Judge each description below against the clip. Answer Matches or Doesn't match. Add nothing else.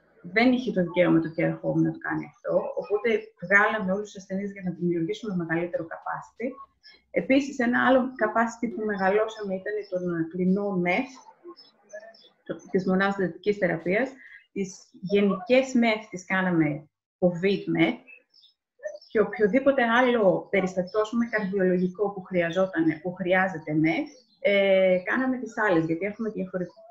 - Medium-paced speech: Matches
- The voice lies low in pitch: Doesn't match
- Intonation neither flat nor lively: Matches